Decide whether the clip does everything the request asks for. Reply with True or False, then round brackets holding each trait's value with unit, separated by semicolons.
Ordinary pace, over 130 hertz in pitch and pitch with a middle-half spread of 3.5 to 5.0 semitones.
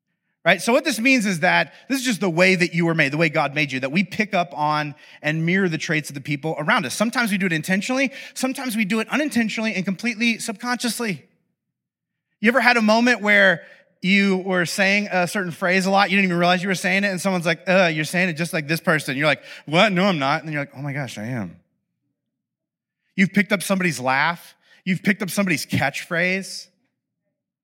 False (230 wpm; 185 Hz; 4.2 semitones)